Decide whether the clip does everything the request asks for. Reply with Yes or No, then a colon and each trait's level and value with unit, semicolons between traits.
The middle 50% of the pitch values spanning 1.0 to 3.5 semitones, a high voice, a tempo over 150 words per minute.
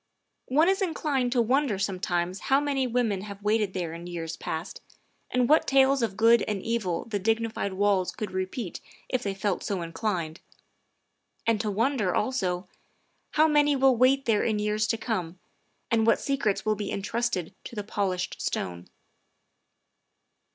No: average, 4.9 semitones; high, 215 Hz; average, 160 wpm